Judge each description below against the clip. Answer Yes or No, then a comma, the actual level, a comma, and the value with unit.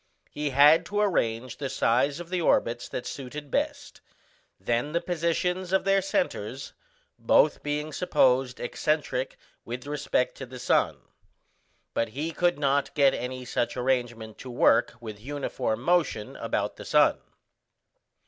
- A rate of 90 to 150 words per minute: Yes, average, 140 wpm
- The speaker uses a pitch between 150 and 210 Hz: No, medium, 140 Hz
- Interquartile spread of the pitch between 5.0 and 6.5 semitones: Yes, wide, 5.4 semitones